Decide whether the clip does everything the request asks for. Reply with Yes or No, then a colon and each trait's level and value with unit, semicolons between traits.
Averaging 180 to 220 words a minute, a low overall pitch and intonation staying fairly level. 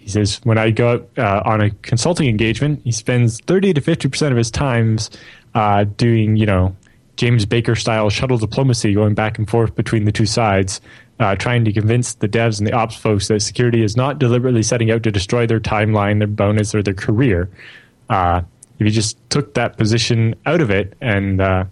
Yes: fast, 205 wpm; low, 110 Hz; narrow, 2.3 semitones